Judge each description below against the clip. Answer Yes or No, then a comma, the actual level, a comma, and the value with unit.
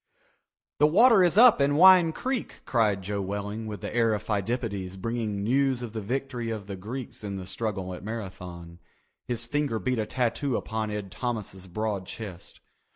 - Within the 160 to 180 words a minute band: Yes, average, 175 wpm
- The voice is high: No, low, 110 Hz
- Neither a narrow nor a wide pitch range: Yes, average, 4.3 semitones